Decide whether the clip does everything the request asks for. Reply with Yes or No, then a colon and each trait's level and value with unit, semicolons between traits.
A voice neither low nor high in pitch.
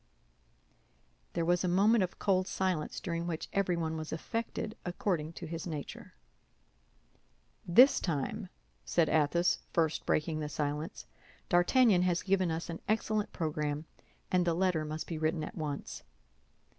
Yes: medium, 170 Hz